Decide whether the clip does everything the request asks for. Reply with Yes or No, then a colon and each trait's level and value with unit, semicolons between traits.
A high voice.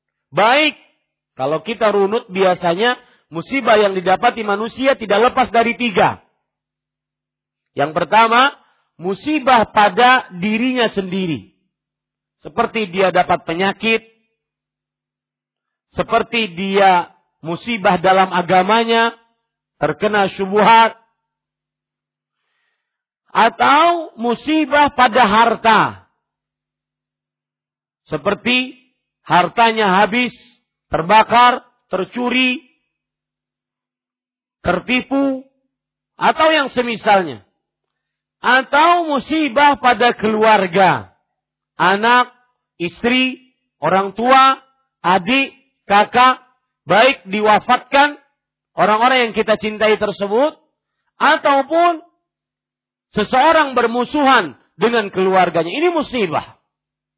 Yes: high, 230 Hz